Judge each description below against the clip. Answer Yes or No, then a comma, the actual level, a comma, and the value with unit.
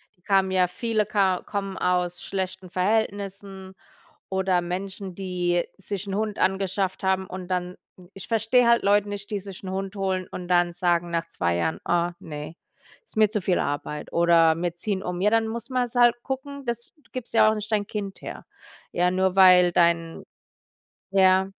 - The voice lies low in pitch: No, high, 190 Hz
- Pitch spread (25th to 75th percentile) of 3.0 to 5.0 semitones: No, narrow, 2.5 semitones